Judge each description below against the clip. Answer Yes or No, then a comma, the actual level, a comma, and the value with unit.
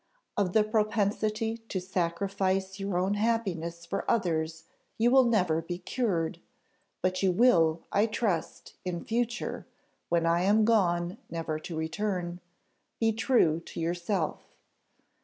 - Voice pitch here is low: No, high, 190 Hz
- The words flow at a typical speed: No, slow, 130 wpm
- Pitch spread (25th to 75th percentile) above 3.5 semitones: Yes, average, 4.2 semitones